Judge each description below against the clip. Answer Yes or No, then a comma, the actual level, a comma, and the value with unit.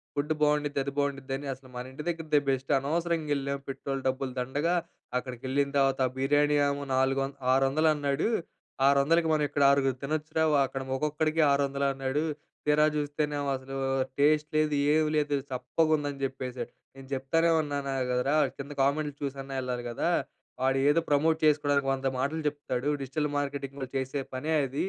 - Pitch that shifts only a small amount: Yes, narrow, 1.8 semitones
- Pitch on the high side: No, medium, 140 Hz